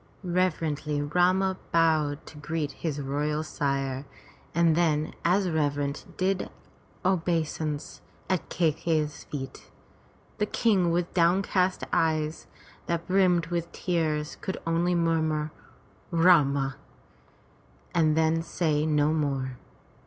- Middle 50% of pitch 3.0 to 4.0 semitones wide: No, narrow, 2.6 semitones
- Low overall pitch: No, medium, 160 Hz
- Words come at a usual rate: No, slow, 110 wpm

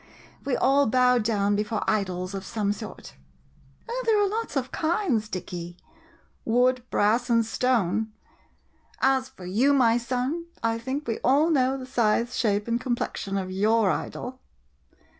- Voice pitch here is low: No, high, 235 Hz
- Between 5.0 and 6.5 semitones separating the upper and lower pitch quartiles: No, average, 3.9 semitones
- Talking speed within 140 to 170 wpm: Yes, average, 155 wpm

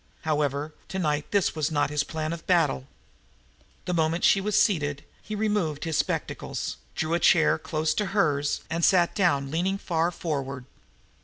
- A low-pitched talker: No, medium, 160 Hz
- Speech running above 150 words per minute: Yes, average, 160 wpm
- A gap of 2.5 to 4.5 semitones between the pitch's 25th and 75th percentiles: Yes, average, 3.5 semitones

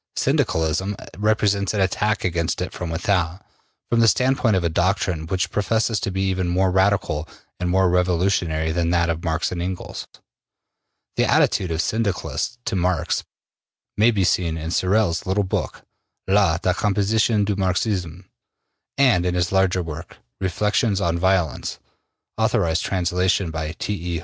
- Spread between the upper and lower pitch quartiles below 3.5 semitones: Yes, average, 3.0 semitones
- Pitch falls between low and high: No, very low, 90 Hz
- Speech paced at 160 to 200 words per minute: No, average, 150 wpm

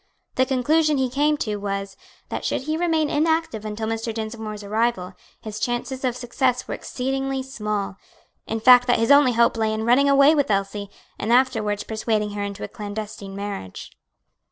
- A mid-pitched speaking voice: No, high, 230 Hz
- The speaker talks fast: No, average, 175 wpm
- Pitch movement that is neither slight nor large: Yes, average, 4.1 semitones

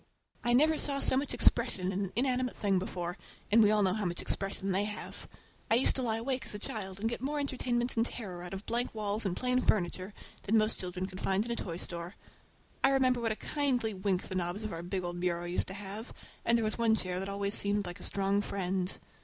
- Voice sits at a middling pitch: No, high, 205 Hz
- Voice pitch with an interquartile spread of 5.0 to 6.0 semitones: No, average, 4.1 semitones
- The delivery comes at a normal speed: No, fast, 245 wpm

